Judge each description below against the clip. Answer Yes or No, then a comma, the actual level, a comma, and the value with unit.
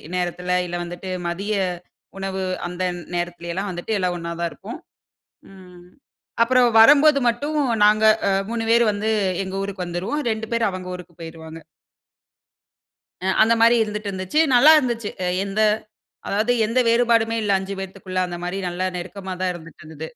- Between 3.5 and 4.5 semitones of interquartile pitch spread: Yes, average, 4.2 semitones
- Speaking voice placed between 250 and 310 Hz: No, high, 195 Hz